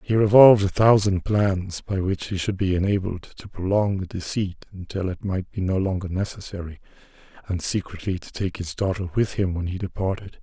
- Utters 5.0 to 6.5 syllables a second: Yes, 5.3 syllables/s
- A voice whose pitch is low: Yes, very low, 95 Hz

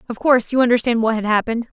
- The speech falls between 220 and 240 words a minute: Yes, fast, 235 wpm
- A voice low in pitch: No, high, 235 Hz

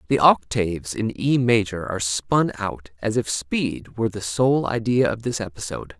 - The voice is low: Yes, low, 110 Hz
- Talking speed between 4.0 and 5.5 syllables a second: Yes, 4.8 syllables/s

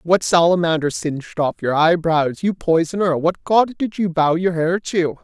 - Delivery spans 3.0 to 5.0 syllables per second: Yes, 4.7 syllables/s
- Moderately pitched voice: Yes, medium, 170 Hz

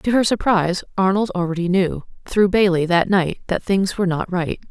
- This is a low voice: No, medium, 185 Hz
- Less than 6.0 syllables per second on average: Yes, 5.3 syllables/s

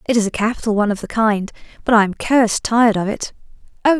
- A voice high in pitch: Yes, high, 220 Hz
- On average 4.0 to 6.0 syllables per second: No, 6.8 syllables/s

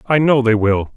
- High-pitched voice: No, low, 125 Hz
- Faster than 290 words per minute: No, fast, 250 wpm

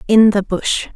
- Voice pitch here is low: No, high, 205 Hz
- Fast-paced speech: No, average, 190 wpm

